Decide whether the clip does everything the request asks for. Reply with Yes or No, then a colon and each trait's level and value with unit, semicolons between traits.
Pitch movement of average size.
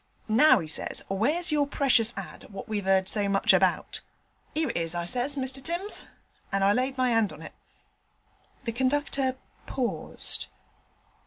No: wide, 5.8 semitones